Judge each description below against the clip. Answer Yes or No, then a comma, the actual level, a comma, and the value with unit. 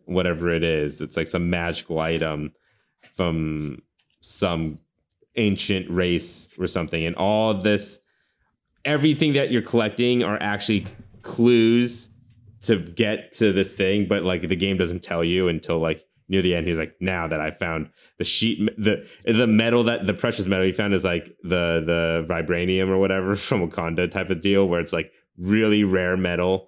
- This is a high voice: No, very low, 95 Hz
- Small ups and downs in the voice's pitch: No, average, 3.9 semitones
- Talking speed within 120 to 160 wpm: No, average, 170 wpm